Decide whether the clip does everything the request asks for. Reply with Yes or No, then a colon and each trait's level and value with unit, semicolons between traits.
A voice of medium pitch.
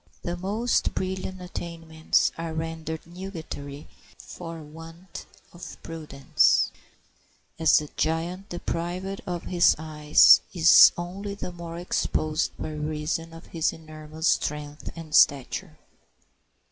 Yes: medium, 165 Hz